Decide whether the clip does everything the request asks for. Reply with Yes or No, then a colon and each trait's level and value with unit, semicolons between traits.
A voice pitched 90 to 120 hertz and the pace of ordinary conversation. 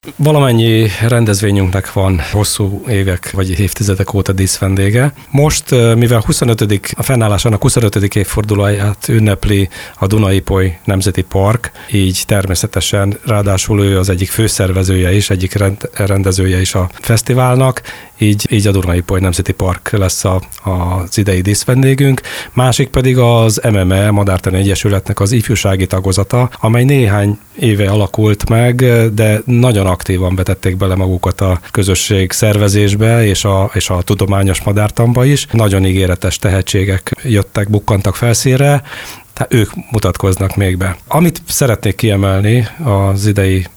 Yes: low, 100 Hz; average, 125 wpm